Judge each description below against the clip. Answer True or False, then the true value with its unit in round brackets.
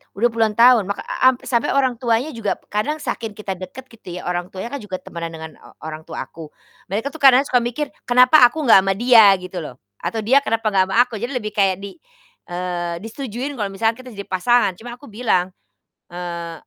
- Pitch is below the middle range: False (215 Hz)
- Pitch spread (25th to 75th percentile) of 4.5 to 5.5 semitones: True (4.8 semitones)